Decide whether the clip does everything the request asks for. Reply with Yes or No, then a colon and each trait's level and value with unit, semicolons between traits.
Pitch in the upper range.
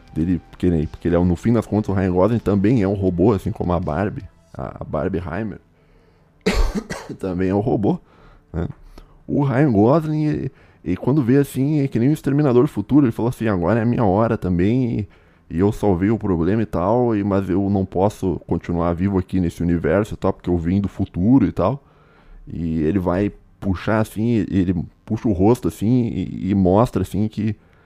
No: low, 100 Hz